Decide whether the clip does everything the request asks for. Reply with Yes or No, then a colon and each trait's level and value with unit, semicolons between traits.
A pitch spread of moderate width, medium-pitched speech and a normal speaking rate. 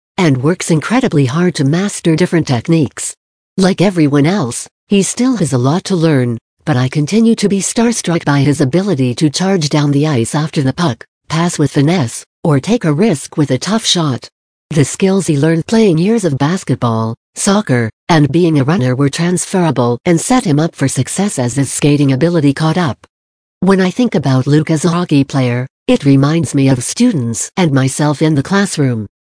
Yes: average, 4.7 semitones; medium, 155 Hz; average, 190 wpm